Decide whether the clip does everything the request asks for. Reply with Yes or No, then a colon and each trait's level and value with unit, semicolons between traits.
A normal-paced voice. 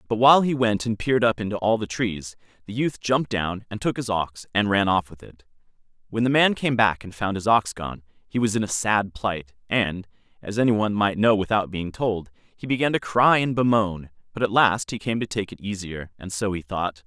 No: fast, 240 wpm